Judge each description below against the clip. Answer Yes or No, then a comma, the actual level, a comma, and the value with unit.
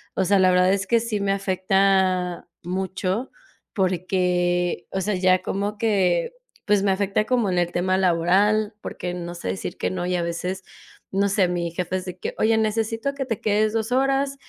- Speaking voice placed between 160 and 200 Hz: Yes, high, 190 Hz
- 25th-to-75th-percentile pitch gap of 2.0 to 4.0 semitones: Yes, average, 2.8 semitones